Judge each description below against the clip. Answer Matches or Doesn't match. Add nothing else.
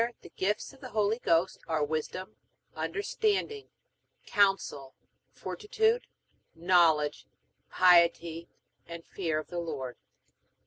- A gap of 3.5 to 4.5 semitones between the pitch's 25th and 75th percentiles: Doesn't match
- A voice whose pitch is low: Doesn't match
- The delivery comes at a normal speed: Doesn't match